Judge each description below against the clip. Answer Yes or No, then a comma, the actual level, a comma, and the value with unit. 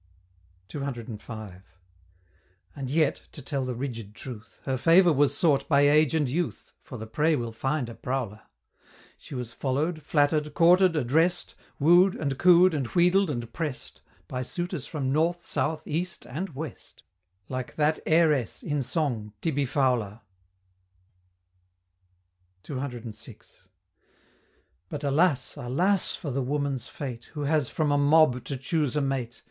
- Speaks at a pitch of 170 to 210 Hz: No, medium, 140 Hz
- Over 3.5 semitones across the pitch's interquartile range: Yes, average, 4.1 semitones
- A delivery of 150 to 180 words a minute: No, average, 140 wpm